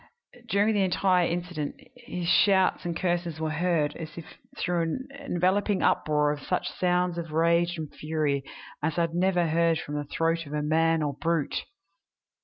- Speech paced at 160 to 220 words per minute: Yes, average, 170 wpm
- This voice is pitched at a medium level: Yes, medium, 170 Hz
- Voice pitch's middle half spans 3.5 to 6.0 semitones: No, narrow, 2.4 semitones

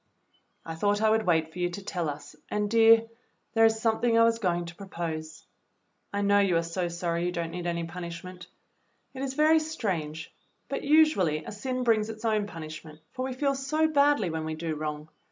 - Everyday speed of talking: No, fast, 210 wpm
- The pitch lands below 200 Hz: Yes, high, 190 Hz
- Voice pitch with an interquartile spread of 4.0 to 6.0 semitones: Yes, wide, 5.4 semitones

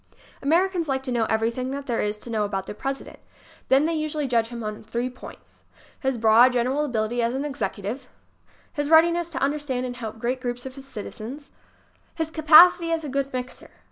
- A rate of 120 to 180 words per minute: No, average, 190 wpm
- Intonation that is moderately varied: Yes, average, 4.0 semitones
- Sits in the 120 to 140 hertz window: No, very high, 255 Hz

